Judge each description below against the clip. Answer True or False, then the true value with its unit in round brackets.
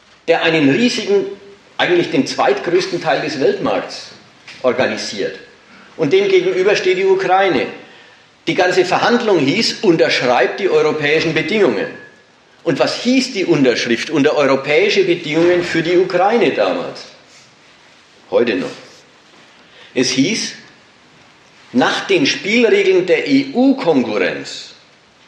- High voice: True (245 Hz)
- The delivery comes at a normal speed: False (105 wpm)